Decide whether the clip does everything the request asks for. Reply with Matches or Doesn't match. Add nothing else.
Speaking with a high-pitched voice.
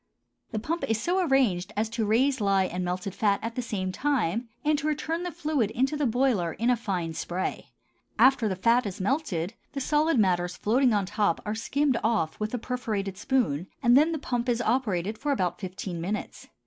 Matches